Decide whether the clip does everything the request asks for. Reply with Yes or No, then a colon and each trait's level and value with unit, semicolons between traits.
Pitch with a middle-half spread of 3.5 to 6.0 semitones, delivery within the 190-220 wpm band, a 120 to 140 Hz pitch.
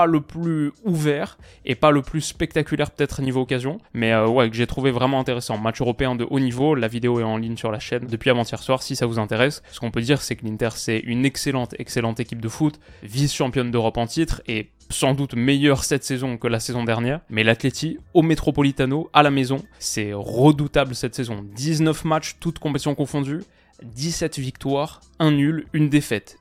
Yes: average, 3.9 semitones; average, 210 wpm; low, 135 Hz